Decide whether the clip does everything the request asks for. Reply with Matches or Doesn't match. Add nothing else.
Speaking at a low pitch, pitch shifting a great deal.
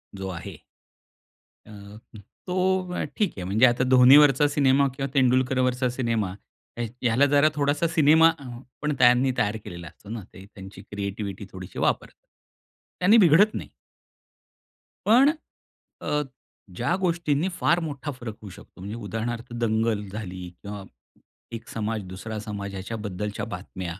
Matches